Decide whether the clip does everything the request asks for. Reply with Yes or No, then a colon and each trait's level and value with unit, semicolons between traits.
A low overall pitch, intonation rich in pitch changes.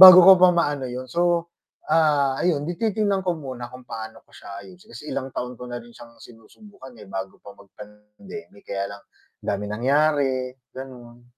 Yes: low, 130 Hz; wide, 6.4 semitones